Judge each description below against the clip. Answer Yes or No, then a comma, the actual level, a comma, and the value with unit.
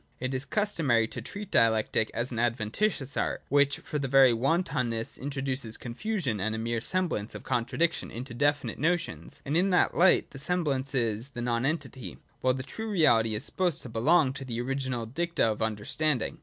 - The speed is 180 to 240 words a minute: Yes, average, 190 wpm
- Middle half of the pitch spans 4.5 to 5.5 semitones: Yes, average, 5.2 semitones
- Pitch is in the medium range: No, low, 130 Hz